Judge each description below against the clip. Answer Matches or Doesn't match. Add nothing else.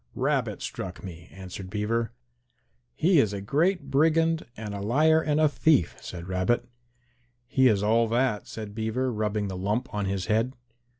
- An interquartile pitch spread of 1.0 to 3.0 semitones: Doesn't match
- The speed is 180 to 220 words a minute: Doesn't match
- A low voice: Matches